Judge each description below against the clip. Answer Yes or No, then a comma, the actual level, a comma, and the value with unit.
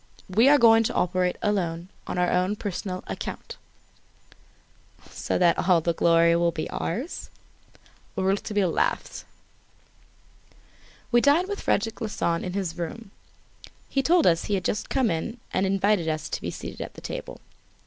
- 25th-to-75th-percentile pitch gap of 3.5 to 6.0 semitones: Yes, average, 4.7 semitones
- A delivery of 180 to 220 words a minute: No, average, 150 wpm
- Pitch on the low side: No, high, 190 Hz